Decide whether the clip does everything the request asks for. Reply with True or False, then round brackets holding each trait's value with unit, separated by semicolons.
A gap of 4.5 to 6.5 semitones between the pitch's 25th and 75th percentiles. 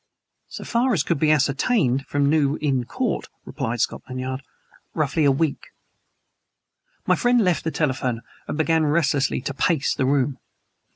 False (3.5 semitones)